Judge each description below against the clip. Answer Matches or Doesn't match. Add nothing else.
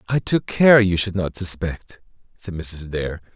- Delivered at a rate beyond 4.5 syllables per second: Doesn't match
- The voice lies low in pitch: Matches